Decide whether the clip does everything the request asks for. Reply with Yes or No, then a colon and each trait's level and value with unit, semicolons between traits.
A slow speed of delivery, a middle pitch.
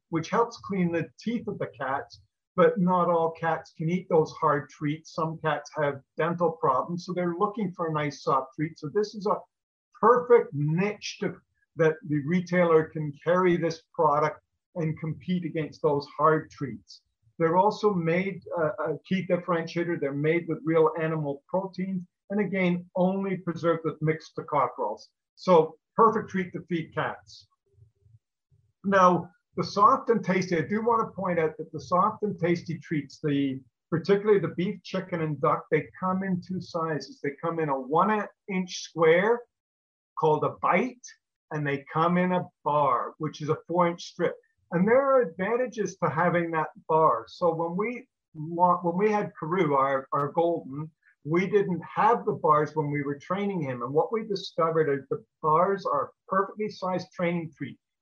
No: average, 175 wpm; medium, 170 Hz